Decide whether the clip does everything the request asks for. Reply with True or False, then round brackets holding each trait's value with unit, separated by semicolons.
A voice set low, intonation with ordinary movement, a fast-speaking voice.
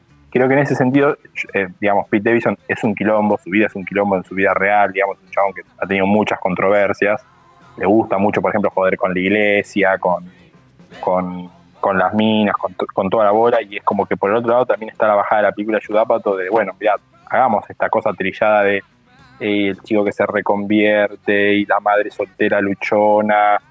False (100 Hz; 1.6 semitones; 210 wpm)